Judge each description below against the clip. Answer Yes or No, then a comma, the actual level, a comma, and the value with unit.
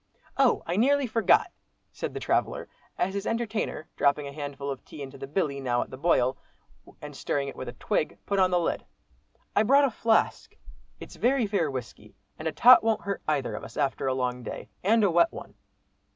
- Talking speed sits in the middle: No, fast, 210 wpm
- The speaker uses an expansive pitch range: Yes, wide, 8.3 semitones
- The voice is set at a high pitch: No, medium, 165 Hz